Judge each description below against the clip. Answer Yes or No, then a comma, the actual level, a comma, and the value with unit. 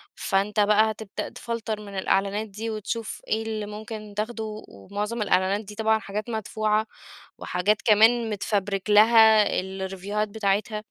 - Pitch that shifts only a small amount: Yes, narrow, 1.6 semitones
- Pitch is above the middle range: Yes, high, 210 Hz